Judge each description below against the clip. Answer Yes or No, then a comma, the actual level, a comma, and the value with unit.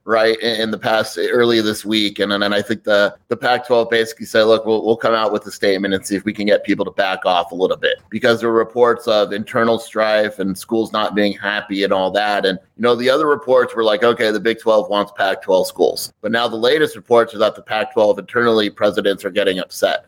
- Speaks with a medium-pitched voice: No, low, 110 Hz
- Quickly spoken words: Yes, fast, 250 wpm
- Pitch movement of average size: No, narrow, 2.0 semitones